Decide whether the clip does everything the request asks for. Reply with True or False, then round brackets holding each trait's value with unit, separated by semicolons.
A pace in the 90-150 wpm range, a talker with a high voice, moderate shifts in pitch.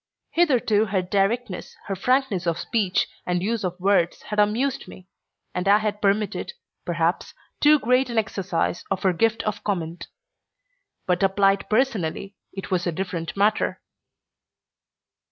True (140 wpm; 200 Hz; 3.3 semitones)